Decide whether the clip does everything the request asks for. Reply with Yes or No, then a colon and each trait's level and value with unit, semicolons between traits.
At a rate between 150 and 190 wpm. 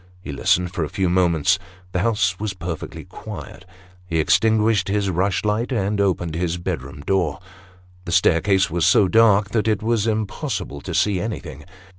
Yes: average, 160 wpm